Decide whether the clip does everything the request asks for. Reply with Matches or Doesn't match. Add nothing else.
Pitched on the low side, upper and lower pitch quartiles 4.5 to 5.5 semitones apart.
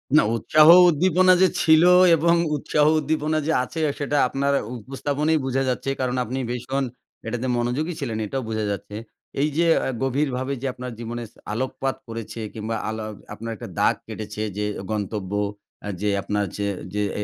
Matches